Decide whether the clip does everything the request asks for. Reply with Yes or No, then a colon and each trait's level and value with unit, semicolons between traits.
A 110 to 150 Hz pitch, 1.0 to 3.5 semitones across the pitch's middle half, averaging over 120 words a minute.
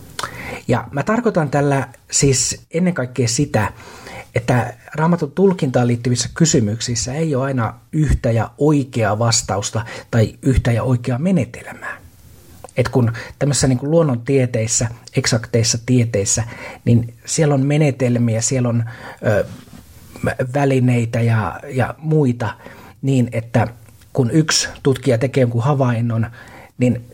No: low, 125 Hz; average, 3.1 semitones; average, 115 wpm